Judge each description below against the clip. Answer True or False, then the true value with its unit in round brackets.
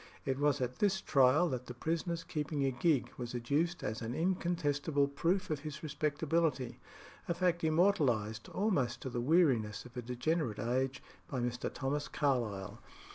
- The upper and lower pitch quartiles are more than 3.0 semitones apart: True (4.9 semitones)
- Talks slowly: False (160 wpm)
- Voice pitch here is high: False (140 Hz)